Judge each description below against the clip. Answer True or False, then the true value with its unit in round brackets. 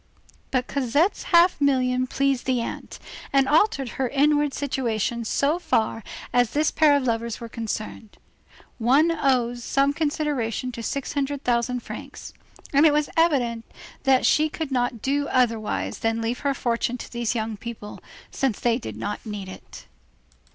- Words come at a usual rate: True (160 wpm)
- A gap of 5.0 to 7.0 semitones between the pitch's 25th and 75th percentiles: False (3.6 semitones)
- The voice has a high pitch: True (255 Hz)